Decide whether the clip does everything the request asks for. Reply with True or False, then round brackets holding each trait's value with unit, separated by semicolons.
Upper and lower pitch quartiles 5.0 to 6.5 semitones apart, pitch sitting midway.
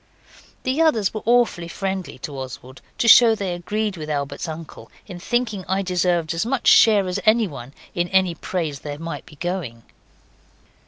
True (5.3 semitones; 180 Hz)